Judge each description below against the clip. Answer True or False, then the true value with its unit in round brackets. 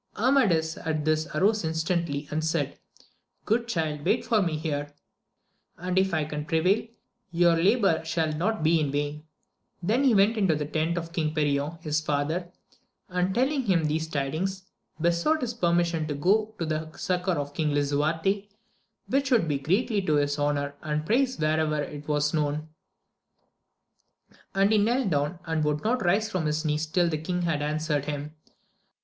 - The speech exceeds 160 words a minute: True (170 wpm)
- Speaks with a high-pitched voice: False (160 Hz)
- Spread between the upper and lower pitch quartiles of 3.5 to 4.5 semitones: True (4.0 semitones)